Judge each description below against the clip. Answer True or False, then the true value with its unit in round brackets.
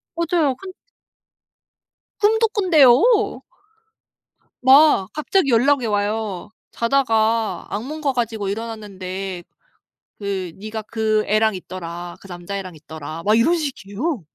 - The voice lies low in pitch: False (220 Hz)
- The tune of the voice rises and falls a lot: True (6.0 semitones)